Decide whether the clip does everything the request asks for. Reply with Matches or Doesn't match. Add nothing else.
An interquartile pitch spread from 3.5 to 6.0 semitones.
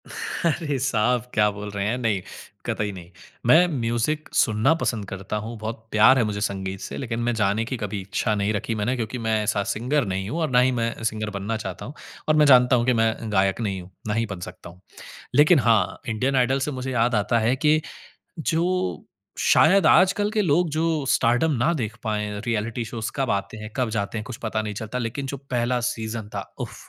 Matches